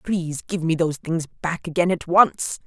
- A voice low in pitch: No, medium, 165 Hz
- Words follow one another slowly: No, fast, 205 wpm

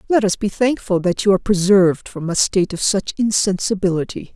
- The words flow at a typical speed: Yes, average, 195 wpm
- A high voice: Yes, high, 195 Hz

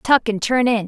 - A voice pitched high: Yes, high, 230 Hz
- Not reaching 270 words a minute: No, fast, 275 wpm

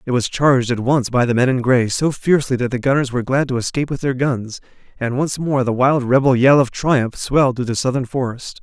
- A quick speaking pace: Yes, fast, 250 wpm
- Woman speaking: No, male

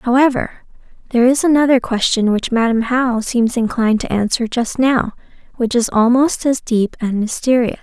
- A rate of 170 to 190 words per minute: No, average, 160 wpm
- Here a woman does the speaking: Yes, female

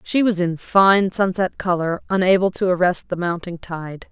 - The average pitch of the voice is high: No, medium, 180 Hz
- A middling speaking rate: Yes, average, 175 wpm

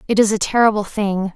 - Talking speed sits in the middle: No, fast, 220 wpm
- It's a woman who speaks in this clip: Yes, female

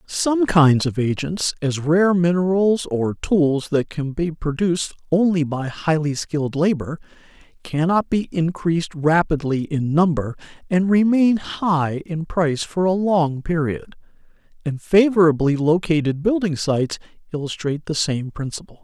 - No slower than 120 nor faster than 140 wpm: Yes, slow, 135 wpm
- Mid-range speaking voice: Yes, medium, 165 Hz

